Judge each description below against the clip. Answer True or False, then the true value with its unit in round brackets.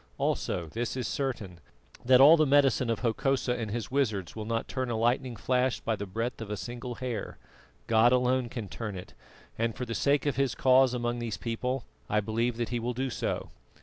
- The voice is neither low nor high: False (120 Hz)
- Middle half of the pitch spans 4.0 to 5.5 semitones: False (2.4 semitones)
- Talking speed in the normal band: False (210 wpm)